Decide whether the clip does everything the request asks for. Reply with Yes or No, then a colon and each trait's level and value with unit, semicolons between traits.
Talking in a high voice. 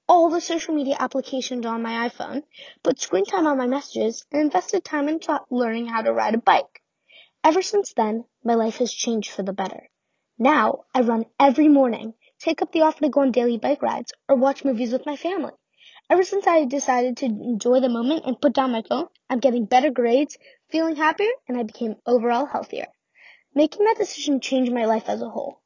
Yes: very high, 270 Hz